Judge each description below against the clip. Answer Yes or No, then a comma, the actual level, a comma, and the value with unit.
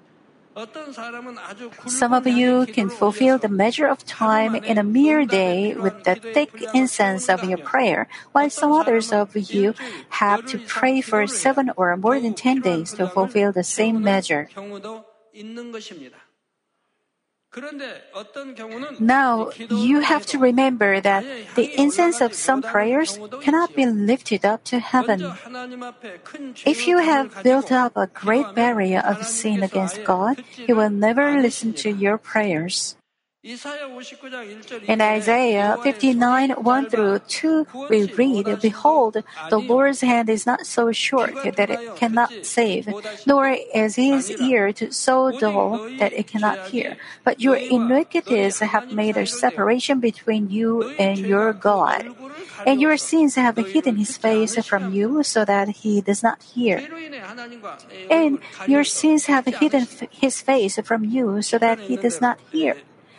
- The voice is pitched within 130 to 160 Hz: No, high, 235 Hz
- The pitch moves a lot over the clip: No, average, 3.8 semitones